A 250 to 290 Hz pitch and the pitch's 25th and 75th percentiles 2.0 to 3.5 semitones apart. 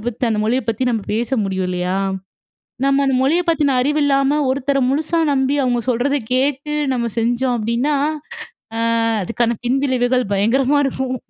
Yes: very high, 255 Hz; average, 2.9 semitones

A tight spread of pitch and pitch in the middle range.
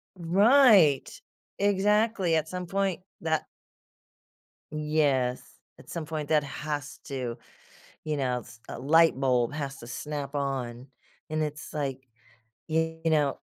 No: average, 3.3 semitones; medium, 150 Hz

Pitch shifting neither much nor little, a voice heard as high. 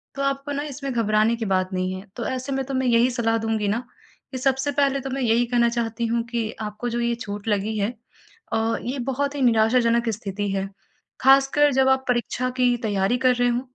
Yes: average, 3.3 semitones; high, 240 Hz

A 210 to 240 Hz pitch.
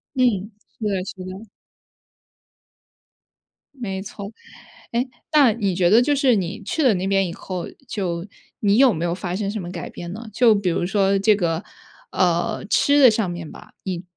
No: high, 195 Hz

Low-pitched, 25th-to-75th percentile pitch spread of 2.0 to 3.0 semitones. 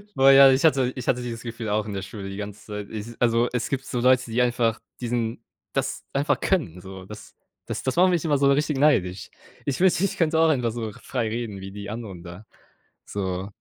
No: low, 120 Hz; average, 4.7 semitones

